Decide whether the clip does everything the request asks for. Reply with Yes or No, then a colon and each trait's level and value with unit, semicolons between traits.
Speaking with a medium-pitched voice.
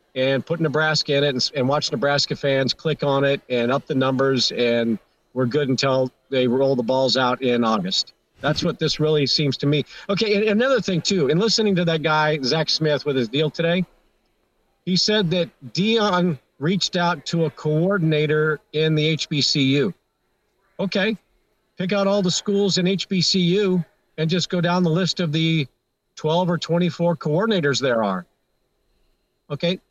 Yes: medium, 155 Hz